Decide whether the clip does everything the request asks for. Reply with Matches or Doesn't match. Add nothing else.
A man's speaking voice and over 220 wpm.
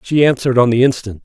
Matches